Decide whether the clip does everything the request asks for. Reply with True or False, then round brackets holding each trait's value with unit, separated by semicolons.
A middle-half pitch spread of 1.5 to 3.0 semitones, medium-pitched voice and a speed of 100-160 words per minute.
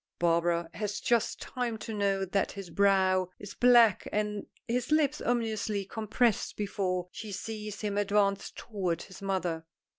False (2.7 semitones; 205 Hz; 145 wpm)